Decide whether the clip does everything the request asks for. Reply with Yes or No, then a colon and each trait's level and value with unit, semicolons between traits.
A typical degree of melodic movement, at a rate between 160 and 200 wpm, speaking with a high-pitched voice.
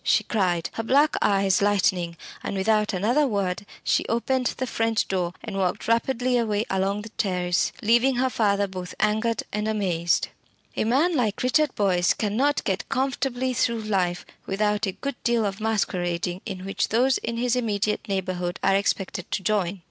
Yes: average, 3.7 semitones; average, 170 wpm; high, 210 Hz